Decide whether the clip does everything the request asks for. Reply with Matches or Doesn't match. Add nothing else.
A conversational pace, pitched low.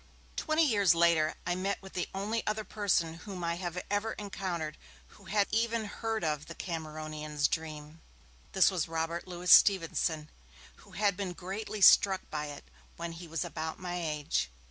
Doesn't match